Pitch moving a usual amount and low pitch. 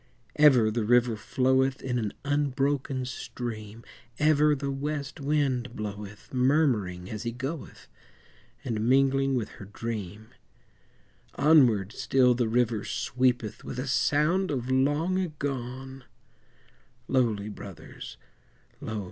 Yes: average, 3.8 semitones; low, 125 Hz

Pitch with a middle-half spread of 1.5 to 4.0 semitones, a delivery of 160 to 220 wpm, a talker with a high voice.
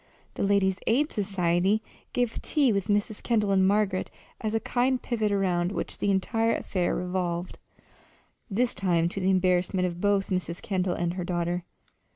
Yes: average, 2.9 semitones; average, 175 wpm; high, 195 Hz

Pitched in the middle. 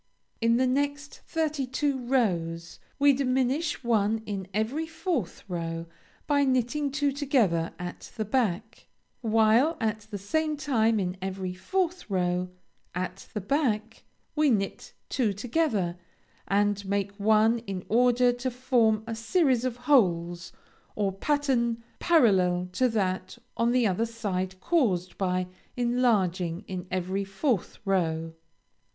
No: high, 225 Hz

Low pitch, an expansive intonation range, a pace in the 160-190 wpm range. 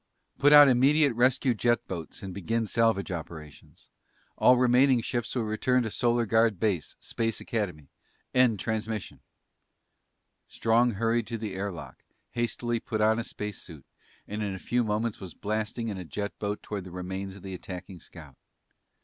No: low, 110 Hz; average, 3.6 semitones; average, 165 wpm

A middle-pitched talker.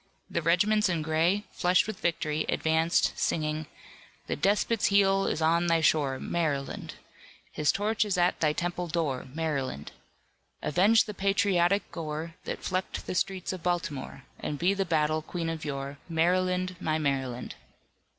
Yes: medium, 170 Hz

